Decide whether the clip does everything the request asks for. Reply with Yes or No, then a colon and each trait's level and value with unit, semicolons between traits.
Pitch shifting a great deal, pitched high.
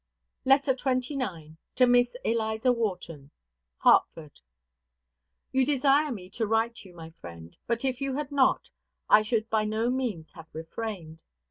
Yes: wide, 6.5 semitones; high, 225 Hz